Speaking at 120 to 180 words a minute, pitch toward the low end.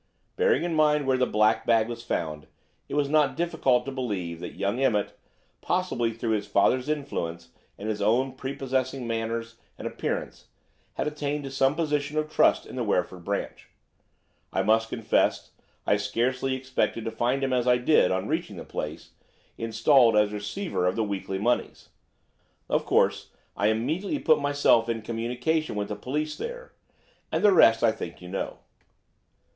Yes: average, 170 wpm; low, 120 Hz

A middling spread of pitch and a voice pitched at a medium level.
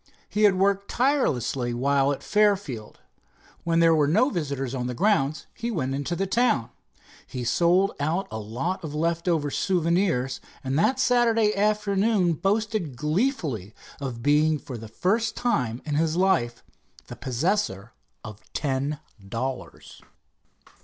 No: wide, 7.2 semitones; medium, 160 Hz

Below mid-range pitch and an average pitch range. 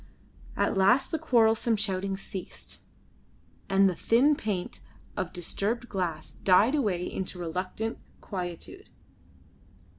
No: high, 195 Hz; average, 3.9 semitones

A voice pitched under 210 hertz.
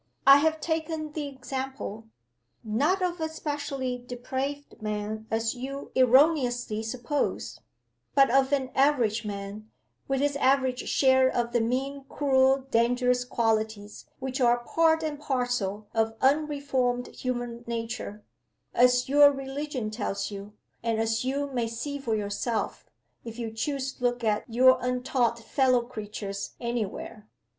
No: very high, 250 Hz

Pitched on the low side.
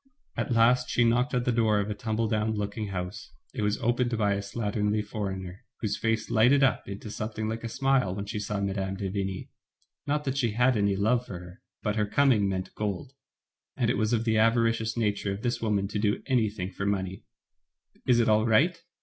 Yes: low, 110 Hz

